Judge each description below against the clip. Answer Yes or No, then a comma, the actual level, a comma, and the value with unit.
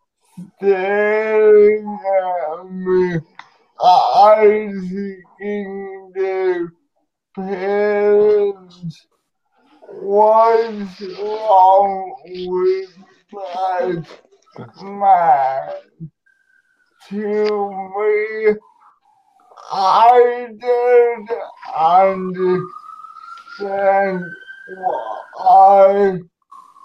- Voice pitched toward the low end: No, high, 205 Hz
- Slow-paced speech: Yes, slow, 40 wpm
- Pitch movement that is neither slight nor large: Yes, average, 4.1 semitones